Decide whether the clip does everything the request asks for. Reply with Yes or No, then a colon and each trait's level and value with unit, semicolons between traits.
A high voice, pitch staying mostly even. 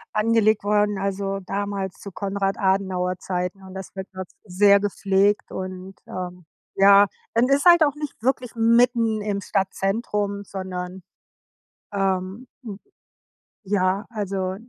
Yes: high, 200 Hz; narrow, 1.9 semitones